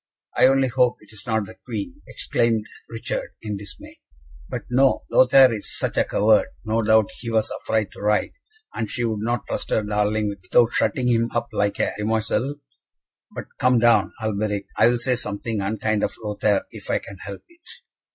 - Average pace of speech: Yes, average, 185 wpm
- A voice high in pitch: No, low, 110 Hz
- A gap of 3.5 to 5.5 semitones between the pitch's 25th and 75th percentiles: No, narrow, 2.5 semitones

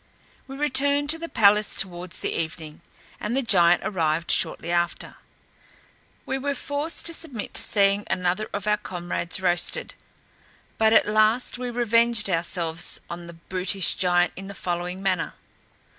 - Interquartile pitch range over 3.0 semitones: Yes, average, 5.2 semitones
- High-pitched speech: Yes, high, 195 Hz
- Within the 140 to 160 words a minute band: Yes, average, 150 wpm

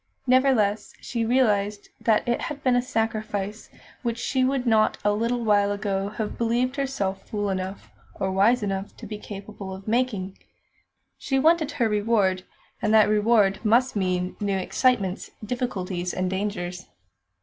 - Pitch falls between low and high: No, high, 210 Hz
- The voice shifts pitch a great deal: No, average, 3.7 semitones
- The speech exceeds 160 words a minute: No, average, 150 wpm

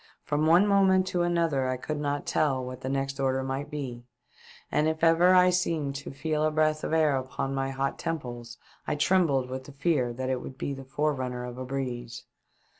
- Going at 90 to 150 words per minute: No, fast, 205 wpm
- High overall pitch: No, medium, 140 Hz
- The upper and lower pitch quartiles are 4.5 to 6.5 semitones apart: No, average, 3.3 semitones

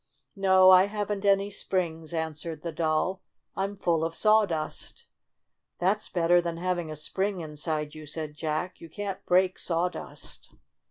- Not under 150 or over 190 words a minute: Yes, average, 160 wpm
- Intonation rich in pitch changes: No, average, 3.2 semitones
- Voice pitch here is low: No, medium, 175 Hz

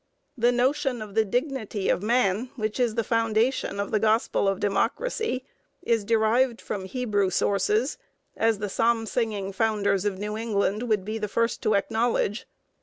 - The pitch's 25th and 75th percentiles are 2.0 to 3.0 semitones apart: Yes, average, 2.7 semitones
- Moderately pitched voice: No, high, 220 Hz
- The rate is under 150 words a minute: No, average, 165 wpm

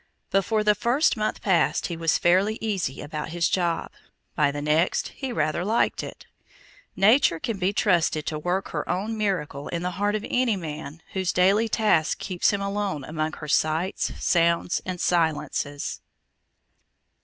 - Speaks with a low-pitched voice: No, medium, 180 Hz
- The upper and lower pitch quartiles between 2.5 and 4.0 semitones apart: No, average, 4.6 semitones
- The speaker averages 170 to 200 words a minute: No, average, 160 wpm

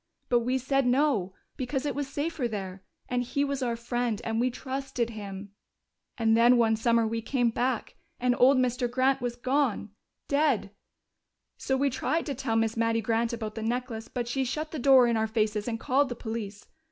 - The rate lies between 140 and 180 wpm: No, average, 195 wpm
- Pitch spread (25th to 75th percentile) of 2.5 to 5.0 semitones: Yes, average, 2.9 semitones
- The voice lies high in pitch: Yes, high, 245 Hz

